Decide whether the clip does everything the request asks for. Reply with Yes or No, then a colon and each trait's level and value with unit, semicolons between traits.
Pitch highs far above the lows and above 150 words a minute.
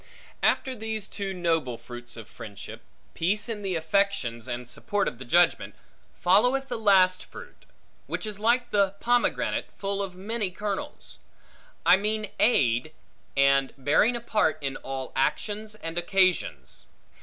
No: wide, 7.5 semitones; average, 145 wpm